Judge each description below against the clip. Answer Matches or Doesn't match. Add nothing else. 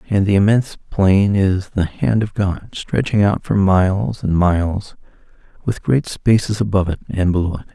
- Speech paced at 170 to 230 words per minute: Matches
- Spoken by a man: Matches